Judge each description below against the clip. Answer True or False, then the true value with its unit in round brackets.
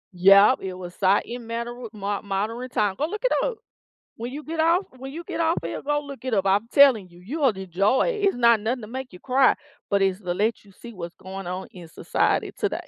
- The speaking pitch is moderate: False (225 Hz)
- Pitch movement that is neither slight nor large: False (5.7 semitones)